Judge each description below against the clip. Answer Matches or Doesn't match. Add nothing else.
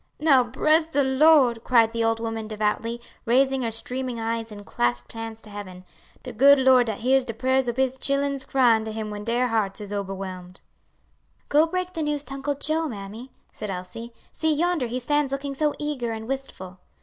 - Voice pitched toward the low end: Doesn't match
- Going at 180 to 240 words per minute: Matches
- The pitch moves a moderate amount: Matches